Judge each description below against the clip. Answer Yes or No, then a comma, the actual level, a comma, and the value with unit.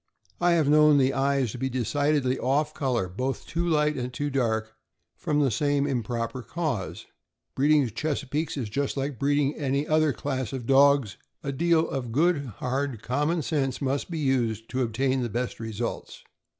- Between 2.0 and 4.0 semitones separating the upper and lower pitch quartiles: Yes, average, 2.9 semitones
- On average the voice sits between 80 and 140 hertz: Yes, low, 135 Hz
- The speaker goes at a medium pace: Yes, average, 175 wpm